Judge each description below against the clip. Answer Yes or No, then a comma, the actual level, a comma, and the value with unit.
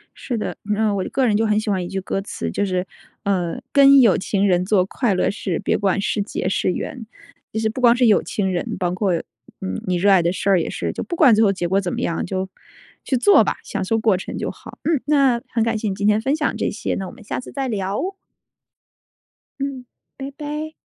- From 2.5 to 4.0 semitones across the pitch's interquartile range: No, average, 4.6 semitones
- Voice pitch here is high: Yes, high, 210 Hz